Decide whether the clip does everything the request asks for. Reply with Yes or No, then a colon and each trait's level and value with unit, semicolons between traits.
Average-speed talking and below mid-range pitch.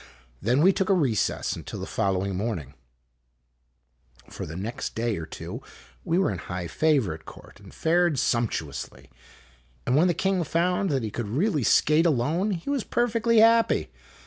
Yes: average, 170 wpm; low, 120 Hz